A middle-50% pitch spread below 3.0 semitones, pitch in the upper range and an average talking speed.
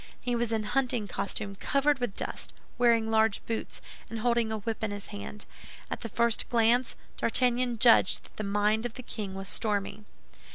Yes: narrow, 2.4 semitones; high, 225 Hz; average, 180 wpm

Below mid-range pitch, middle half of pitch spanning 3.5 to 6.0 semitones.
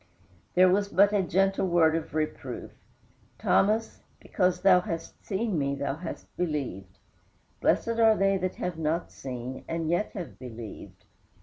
No: medium, 175 Hz; average, 4.3 semitones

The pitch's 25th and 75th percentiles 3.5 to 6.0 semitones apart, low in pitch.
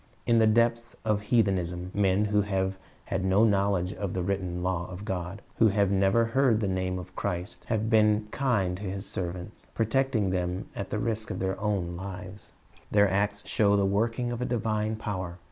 No: average, 2.7 semitones; low, 100 Hz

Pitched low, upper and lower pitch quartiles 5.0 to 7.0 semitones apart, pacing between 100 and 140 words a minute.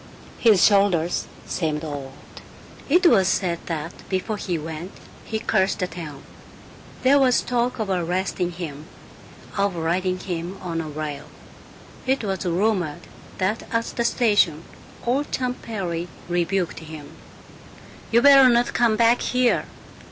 No: medium, 185 Hz; wide, 5.6 semitones; slow, 135 wpm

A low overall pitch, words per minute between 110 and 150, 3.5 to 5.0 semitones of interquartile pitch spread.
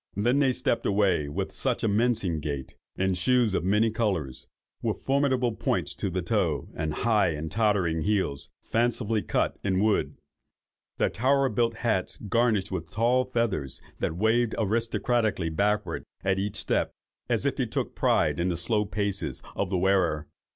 No: low, 105 Hz; average, 165 wpm; average, 4.2 semitones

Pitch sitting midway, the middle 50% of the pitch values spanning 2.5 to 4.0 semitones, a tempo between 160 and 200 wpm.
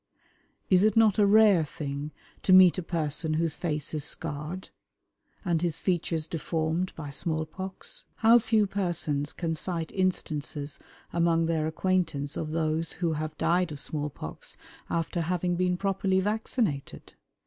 No: medium, 165 Hz; average, 3.2 semitones; average, 150 wpm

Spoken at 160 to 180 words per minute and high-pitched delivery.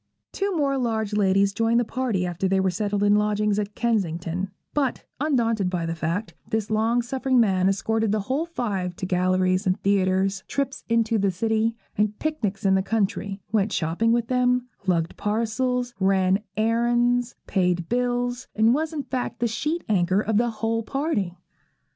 Yes: average, 170 wpm; high, 215 Hz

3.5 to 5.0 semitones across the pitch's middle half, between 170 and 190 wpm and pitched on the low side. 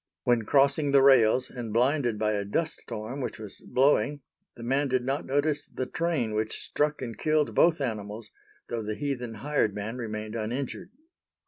Yes: average, 4.5 semitones; average, 175 wpm; low, 125 Hz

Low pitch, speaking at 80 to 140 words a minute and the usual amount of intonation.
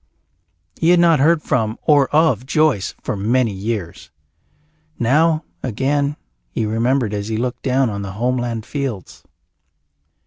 Yes: low, 125 Hz; slow, 135 wpm; average, 5.0 semitones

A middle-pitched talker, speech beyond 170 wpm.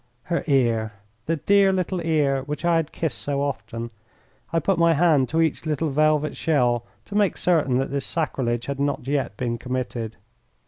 Yes: medium, 145 Hz; average, 180 wpm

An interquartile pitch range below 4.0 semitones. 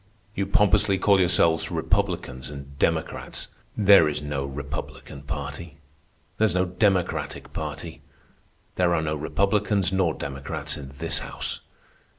No: average, 5.1 semitones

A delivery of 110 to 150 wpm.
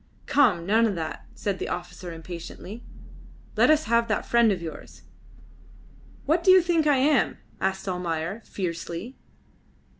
Yes: average, 145 wpm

